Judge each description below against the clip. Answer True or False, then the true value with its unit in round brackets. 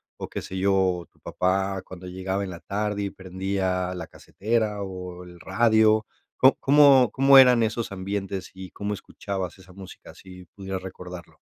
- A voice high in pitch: False (95 Hz)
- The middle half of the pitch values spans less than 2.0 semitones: False (2.3 semitones)